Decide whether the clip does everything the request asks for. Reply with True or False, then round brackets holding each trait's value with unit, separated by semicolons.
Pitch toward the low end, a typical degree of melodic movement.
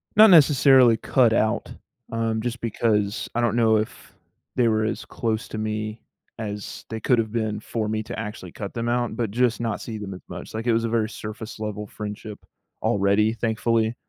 False (110 Hz; 1.6 semitones)